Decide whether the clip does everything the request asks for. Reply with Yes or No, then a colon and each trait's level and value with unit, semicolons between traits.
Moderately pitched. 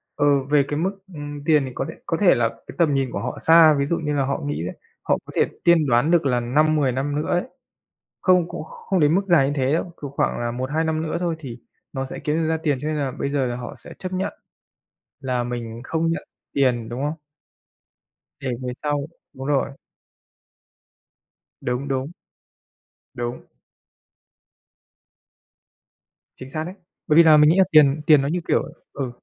Yes: medium, 145 Hz